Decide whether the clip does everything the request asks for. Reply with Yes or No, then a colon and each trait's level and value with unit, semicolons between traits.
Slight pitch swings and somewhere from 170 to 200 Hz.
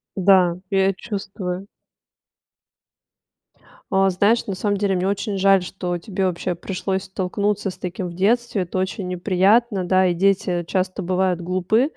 Yes: narrow, 1.7 semitones; high, 190 Hz